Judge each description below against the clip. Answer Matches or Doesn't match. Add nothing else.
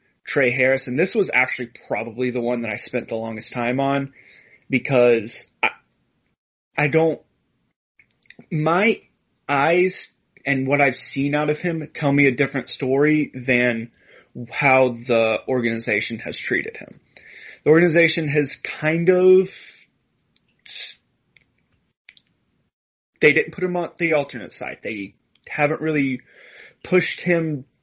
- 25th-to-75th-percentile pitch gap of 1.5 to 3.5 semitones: Doesn't match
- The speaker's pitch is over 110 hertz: Matches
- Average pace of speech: Doesn't match